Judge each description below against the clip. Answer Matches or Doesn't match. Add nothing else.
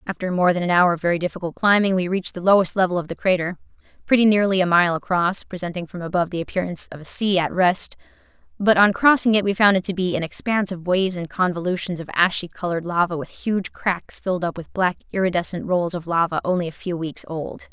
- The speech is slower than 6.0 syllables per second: Doesn't match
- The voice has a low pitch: Doesn't match